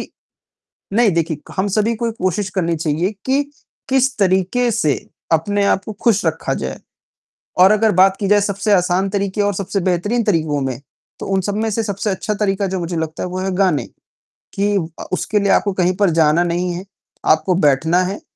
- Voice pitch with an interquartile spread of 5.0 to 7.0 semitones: No, average, 3.0 semitones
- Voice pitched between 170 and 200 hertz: Yes, high, 190 Hz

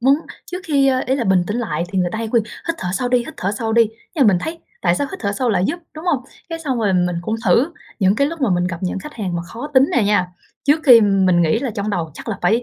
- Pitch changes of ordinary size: No, wide, 6.2 semitones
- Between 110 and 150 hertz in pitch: No, high, 225 Hz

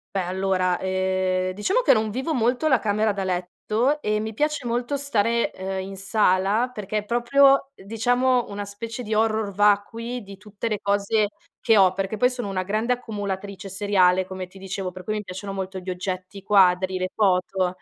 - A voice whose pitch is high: Yes, high, 205 Hz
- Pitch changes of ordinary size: Yes, average, 3.4 semitones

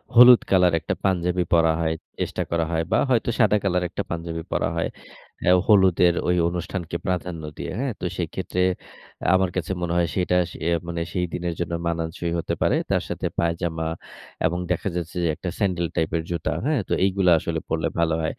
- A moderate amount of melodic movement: No, narrow, 1.8 semitones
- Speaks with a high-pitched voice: No, very low, 85 Hz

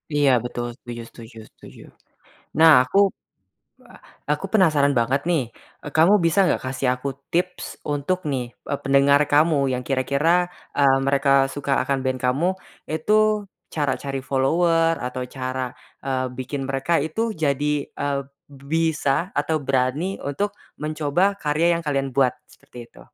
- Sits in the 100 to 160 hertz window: Yes, medium, 140 Hz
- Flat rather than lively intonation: No, average, 3.6 semitones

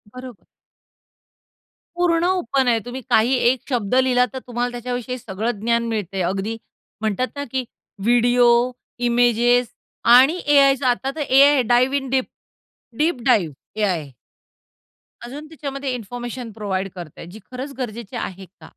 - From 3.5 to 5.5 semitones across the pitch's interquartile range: No, average, 3.0 semitones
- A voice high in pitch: Yes, high, 245 Hz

